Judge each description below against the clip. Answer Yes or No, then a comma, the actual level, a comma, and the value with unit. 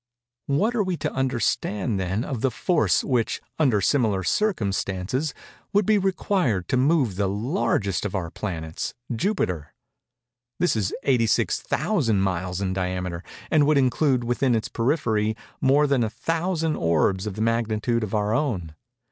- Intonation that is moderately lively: No, wide, 6.9 semitones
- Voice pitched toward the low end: Yes, low, 115 Hz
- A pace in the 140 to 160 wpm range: Yes, average, 150 wpm